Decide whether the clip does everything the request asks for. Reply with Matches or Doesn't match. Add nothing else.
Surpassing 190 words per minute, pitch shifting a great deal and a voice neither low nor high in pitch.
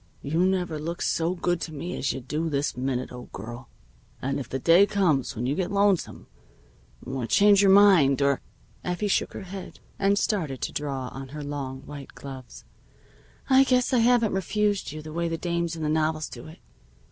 Matches